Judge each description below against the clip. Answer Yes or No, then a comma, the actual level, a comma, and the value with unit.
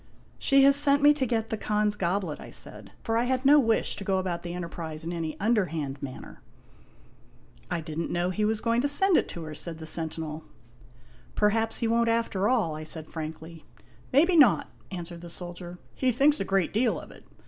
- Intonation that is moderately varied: No, wide, 6.2 semitones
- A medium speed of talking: No, fast, 220 wpm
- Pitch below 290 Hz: Yes, high, 190 Hz